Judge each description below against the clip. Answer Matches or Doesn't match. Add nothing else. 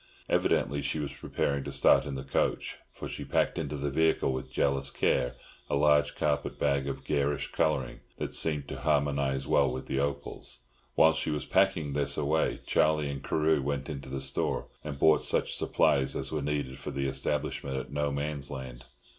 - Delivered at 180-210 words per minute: Matches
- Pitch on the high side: Doesn't match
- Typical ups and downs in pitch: Doesn't match